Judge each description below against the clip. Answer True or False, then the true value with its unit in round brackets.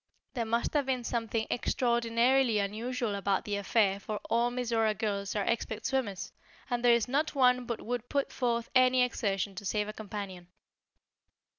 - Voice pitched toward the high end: True (230 Hz)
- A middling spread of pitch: True (3.0 semitones)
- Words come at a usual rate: True (165 wpm)